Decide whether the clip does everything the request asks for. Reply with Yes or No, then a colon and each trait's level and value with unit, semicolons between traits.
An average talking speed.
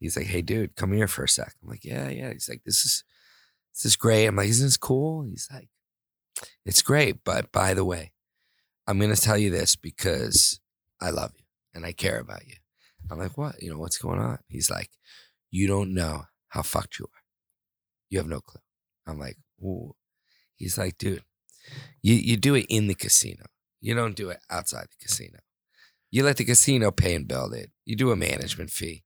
No: fast, 210 wpm